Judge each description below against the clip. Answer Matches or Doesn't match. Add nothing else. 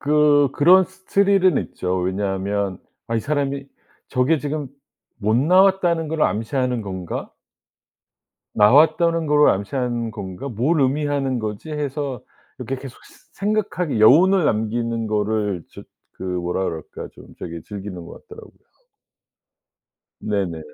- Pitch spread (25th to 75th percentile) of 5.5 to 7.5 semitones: Matches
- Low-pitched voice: Matches